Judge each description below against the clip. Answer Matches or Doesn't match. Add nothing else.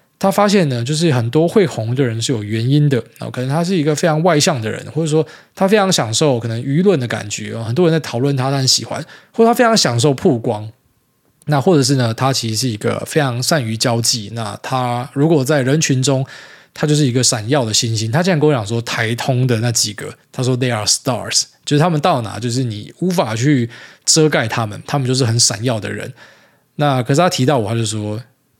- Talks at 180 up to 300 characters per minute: Doesn't match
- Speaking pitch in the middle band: Doesn't match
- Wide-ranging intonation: Doesn't match